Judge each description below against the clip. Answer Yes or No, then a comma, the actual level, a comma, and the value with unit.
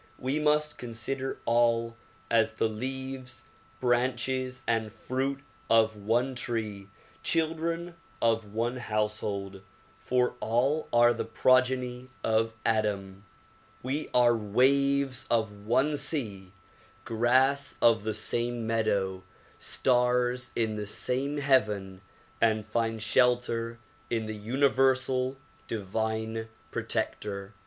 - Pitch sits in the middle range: No, low, 120 Hz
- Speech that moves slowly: Yes, slow, 105 wpm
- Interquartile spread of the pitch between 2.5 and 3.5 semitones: Yes, average, 3.0 semitones